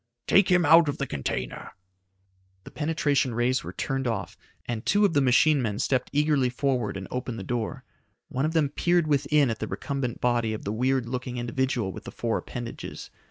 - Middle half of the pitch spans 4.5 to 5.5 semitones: No, average, 3.6 semitones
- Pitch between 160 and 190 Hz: No, low, 130 Hz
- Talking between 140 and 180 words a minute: No, average, 195 wpm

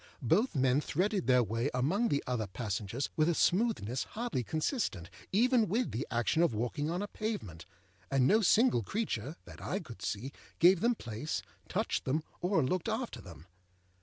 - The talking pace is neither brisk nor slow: Yes, average, 170 wpm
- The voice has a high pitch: No, medium, 150 Hz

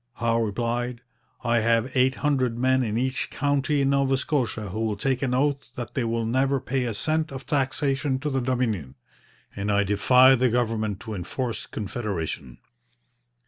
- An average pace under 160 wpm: No, average, 170 wpm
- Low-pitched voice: Yes, low, 125 Hz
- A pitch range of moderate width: Yes, average, 3.1 semitones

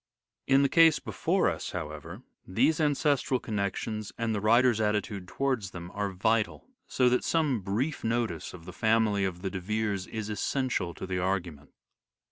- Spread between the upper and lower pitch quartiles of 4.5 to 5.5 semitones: Yes, average, 4.9 semitones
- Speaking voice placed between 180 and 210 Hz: No, low, 105 Hz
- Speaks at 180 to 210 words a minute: No, average, 165 wpm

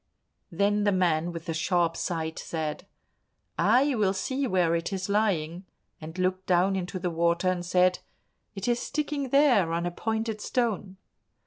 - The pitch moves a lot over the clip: No, average, 3.7 semitones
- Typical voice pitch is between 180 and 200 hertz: Yes, medium, 185 Hz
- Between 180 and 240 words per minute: No, average, 160 wpm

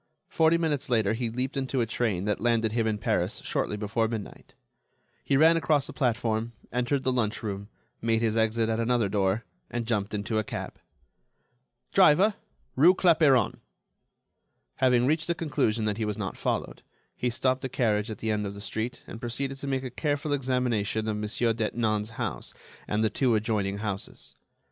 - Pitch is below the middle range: Yes, low, 115 Hz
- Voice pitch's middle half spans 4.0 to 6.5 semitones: No, average, 3.5 semitones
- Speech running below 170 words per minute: No, average, 175 wpm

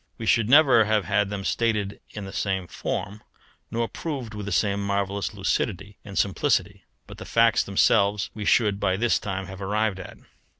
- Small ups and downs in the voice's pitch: Yes, narrow, 2.0 semitones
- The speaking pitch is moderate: No, low, 100 Hz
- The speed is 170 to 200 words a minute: Yes, average, 180 wpm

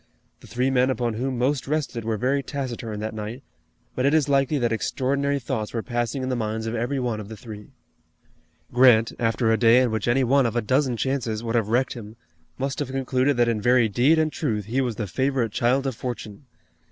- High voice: No, low, 125 Hz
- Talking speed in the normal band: No, fast, 220 wpm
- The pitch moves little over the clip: No, average, 3.0 semitones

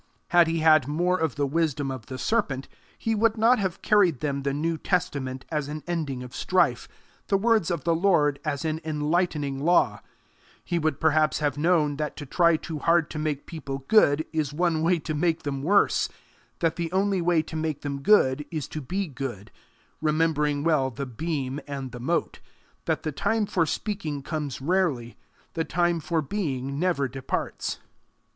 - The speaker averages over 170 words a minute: Yes, average, 180 wpm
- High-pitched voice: No, medium, 155 Hz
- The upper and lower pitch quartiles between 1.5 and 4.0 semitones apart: Yes, average, 3.6 semitones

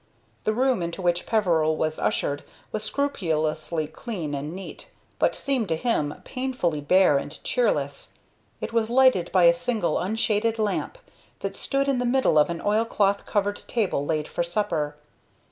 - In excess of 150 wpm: Yes, average, 160 wpm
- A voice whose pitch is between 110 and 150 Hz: No, high, 190 Hz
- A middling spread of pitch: No, wide, 6.5 semitones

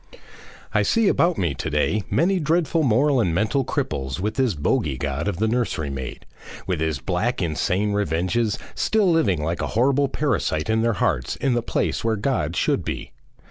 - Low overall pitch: Yes, low, 105 Hz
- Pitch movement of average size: No, wide, 8.8 semitones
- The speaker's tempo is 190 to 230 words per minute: No, average, 180 wpm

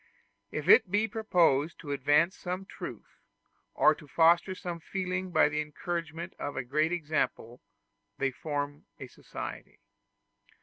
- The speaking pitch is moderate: Yes, medium, 165 Hz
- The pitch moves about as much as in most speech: Yes, average, 3.7 semitones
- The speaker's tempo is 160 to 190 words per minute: No, slow, 135 wpm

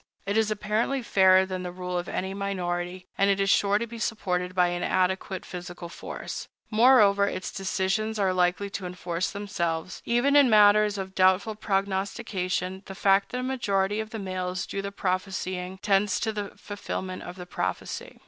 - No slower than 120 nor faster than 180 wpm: Yes, average, 175 wpm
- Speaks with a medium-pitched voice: No, high, 195 Hz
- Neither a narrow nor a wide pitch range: No, narrow, 2.2 semitones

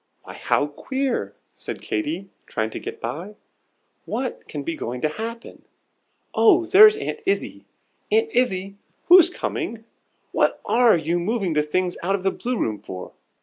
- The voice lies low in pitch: No, high, 210 Hz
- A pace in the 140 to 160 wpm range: Yes, average, 155 wpm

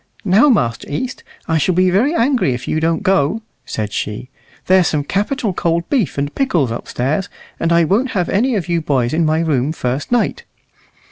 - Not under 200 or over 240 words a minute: No, average, 185 wpm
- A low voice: No, medium, 165 Hz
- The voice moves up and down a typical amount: No, wide, 5.9 semitones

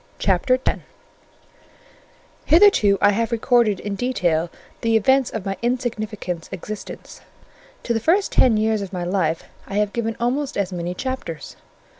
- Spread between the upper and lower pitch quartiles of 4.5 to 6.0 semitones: No, average, 4.1 semitones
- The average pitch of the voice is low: No, high, 215 Hz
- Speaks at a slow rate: No, average, 145 wpm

